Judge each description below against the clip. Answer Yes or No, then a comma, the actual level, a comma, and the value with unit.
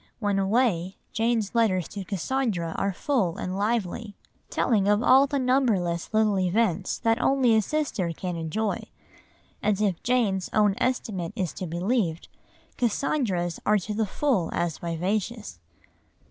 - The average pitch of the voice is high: Yes, high, 205 Hz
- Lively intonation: No, average, 4.3 semitones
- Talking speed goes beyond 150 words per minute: No, average, 145 wpm